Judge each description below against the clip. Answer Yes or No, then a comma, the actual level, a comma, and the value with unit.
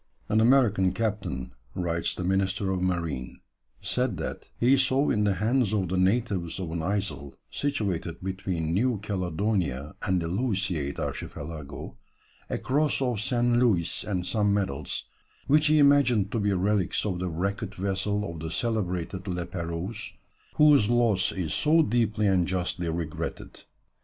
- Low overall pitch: Yes, very low, 95 Hz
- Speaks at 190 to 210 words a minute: No, average, 150 wpm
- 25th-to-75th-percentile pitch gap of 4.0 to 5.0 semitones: Yes, average, 4.4 semitones